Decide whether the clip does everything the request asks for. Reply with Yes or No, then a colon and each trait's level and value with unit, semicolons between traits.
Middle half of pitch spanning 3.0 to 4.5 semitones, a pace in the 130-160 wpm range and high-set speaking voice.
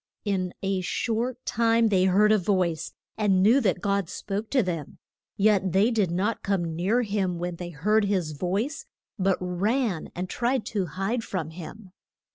No: average, 3.4 semitones; average, 170 wpm; high, 195 Hz